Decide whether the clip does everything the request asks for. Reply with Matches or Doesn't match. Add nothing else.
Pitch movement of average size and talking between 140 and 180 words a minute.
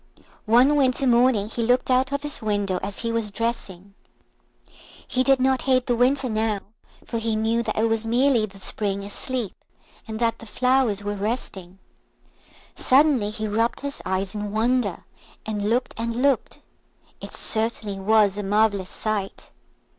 Matches